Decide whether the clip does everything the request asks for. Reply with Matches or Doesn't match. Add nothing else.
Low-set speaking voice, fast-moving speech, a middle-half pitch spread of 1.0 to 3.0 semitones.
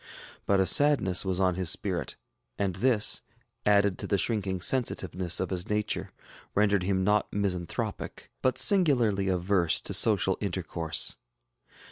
Doesn't match